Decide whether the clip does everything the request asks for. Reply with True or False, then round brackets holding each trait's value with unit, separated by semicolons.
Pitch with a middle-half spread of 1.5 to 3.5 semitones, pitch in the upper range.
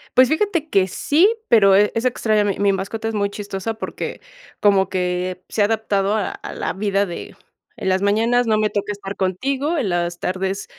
True (2.8 semitones; 205 Hz)